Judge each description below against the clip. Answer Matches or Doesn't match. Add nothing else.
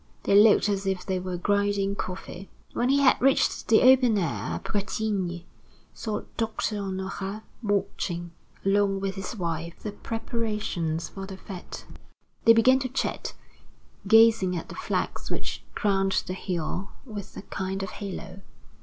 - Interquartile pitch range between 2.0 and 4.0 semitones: Matches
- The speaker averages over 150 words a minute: Doesn't match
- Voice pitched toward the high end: Matches